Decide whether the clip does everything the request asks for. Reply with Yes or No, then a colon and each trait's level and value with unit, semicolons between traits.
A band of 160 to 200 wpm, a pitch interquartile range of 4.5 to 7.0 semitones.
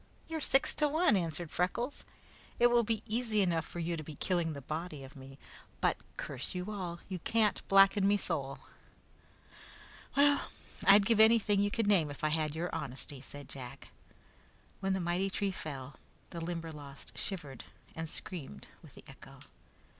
Yes: average, 170 wpm; average, 5.2 semitones